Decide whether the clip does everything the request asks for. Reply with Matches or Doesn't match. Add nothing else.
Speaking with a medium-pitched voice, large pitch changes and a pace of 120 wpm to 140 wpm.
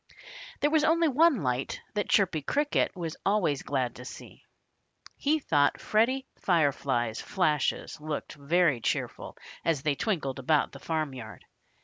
Matches